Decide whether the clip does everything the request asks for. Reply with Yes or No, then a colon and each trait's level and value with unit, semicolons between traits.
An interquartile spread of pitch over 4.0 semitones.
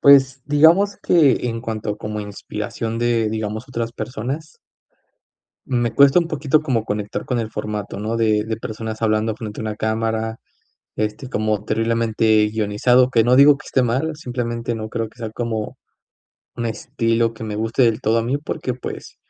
No: narrow, 2.6 semitones